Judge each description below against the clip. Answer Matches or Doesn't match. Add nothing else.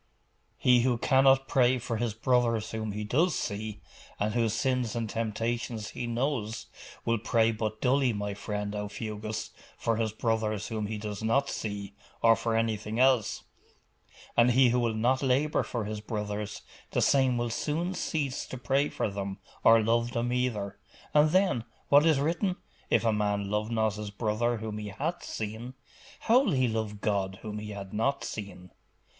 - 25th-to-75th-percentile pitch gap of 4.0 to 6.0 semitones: Doesn't match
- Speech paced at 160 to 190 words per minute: Matches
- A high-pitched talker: Doesn't match